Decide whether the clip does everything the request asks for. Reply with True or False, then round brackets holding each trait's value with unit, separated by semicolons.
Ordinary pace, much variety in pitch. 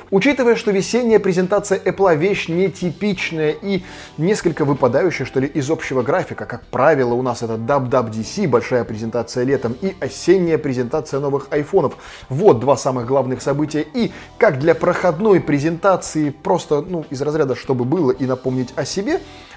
True (150 wpm; 6.0 semitones)